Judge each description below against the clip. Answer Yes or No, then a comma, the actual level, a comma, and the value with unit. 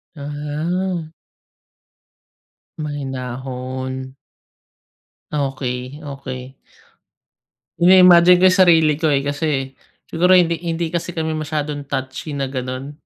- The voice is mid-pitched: Yes, medium, 145 Hz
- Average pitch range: Yes, average, 3.7 semitones